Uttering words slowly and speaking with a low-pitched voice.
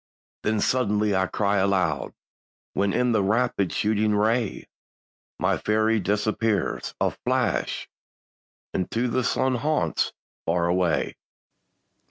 Yes: slow, 110 wpm; low, 105 Hz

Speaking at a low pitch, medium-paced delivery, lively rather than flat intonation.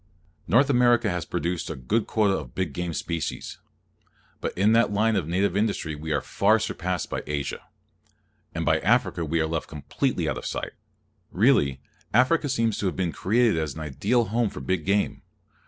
Yes: very low, 95 Hz; average, 185 wpm; wide, 5.8 semitones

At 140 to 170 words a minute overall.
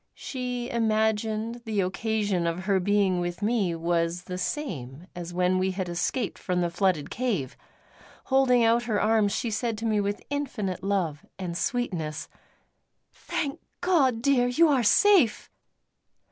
Yes: average, 145 wpm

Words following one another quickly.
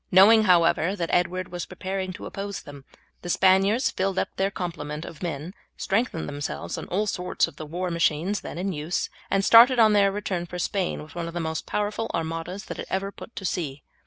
Yes: fast, 210 wpm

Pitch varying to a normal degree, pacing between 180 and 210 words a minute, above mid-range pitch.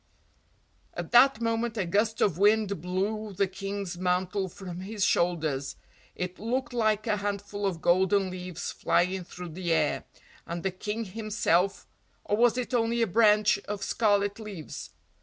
No: average, 3.1 semitones; average, 155 wpm; high, 200 Hz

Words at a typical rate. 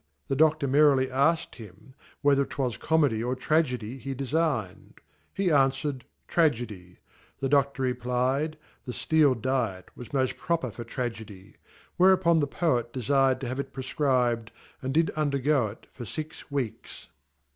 Yes: average, 145 wpm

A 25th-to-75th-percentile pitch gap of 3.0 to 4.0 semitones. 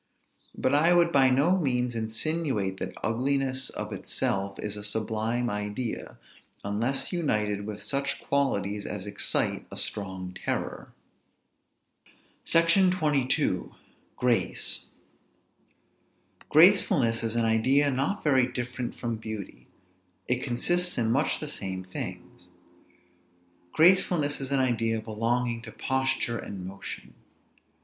No: average, 4.7 semitones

